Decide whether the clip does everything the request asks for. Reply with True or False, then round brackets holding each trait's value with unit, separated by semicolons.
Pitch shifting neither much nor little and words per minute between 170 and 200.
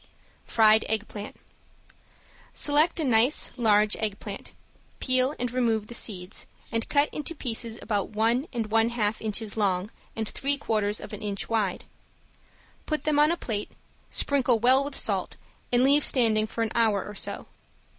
False (3.4 semitones; 155 wpm)